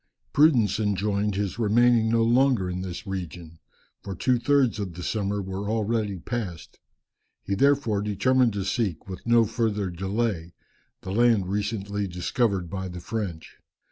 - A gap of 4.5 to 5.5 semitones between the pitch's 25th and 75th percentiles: No, average, 3.6 semitones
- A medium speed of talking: Yes, average, 145 wpm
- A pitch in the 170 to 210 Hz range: No, low, 105 Hz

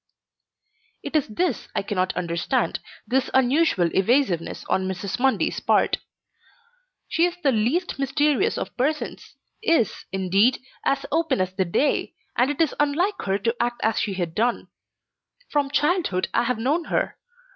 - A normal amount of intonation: No, wide, 7.4 semitones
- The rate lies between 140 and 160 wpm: Yes, average, 150 wpm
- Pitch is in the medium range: No, very high, 250 Hz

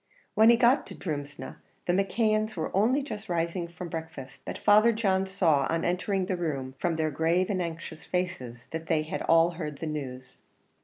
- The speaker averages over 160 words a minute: Yes, average, 190 wpm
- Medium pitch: Yes, medium, 170 Hz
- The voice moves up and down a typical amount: Yes, average, 3.9 semitones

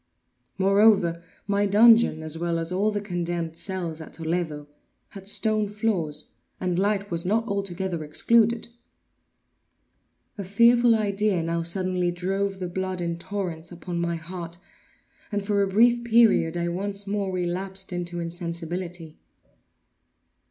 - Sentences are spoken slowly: Yes, slow, 130 wpm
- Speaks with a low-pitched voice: No, medium, 185 Hz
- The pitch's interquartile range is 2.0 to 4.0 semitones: Yes, average, 3.0 semitones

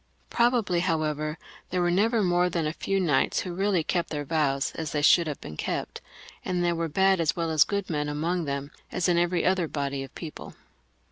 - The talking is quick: Yes, fast, 215 wpm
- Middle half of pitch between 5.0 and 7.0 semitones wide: No, average, 3.2 semitones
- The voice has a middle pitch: Yes, medium, 170 Hz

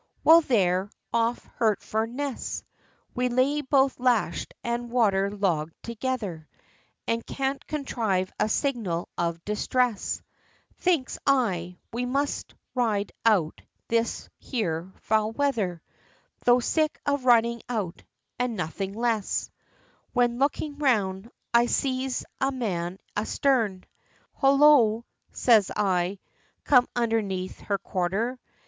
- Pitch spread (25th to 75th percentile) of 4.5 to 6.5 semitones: Yes, average, 4.8 semitones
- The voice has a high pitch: Yes, high, 230 Hz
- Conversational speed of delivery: No, slow, 115 wpm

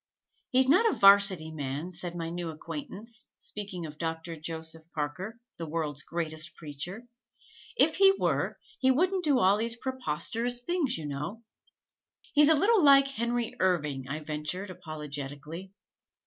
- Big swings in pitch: Yes, wide, 7.7 semitones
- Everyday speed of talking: Yes, average, 145 wpm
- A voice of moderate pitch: Yes, medium, 180 Hz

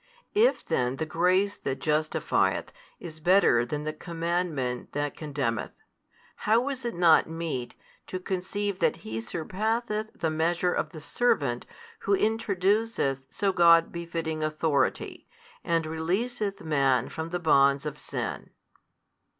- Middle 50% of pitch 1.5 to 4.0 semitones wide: No, average, 4.5 semitones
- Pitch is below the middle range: No, medium, 165 Hz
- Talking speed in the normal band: No, slow, 130 wpm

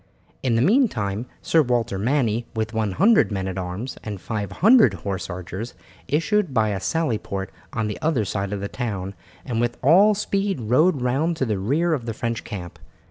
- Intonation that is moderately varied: No, wide, 7.2 semitones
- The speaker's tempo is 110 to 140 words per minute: No, average, 185 wpm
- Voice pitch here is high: No, low, 115 Hz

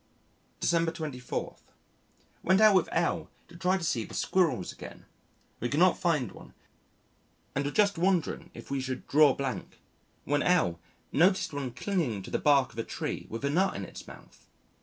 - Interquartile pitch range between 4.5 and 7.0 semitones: Yes, wide, 5.5 semitones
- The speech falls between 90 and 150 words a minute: No, average, 180 wpm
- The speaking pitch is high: No, medium, 155 Hz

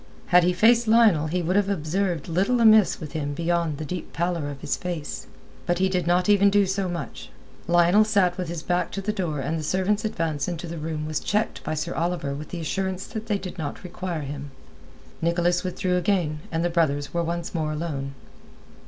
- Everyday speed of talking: No, fast, 210 wpm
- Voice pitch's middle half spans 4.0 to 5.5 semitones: No, average, 3.4 semitones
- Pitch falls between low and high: Yes, medium, 175 Hz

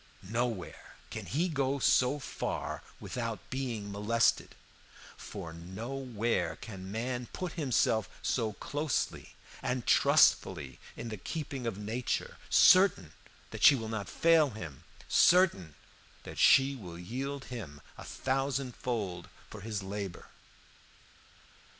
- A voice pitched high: No, low, 115 Hz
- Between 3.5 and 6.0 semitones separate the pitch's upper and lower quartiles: Yes, average, 5.0 semitones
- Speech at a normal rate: No, slow, 120 wpm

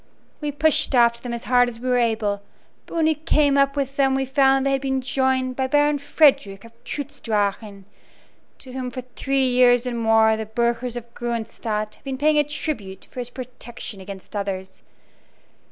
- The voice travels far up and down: No, average, 3.5 semitones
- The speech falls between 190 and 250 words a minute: Yes, average, 195 wpm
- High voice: Yes, very high, 250 Hz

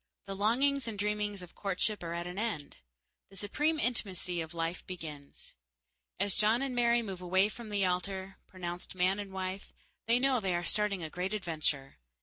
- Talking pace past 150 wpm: Yes, average, 180 wpm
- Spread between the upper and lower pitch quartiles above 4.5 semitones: No, average, 3.2 semitones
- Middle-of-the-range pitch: No, high, 195 Hz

